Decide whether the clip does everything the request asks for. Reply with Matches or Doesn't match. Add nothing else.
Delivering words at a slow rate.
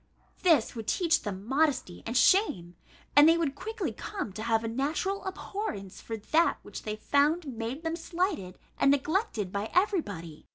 Doesn't match